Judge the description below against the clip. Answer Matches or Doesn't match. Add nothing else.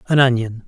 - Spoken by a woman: Doesn't match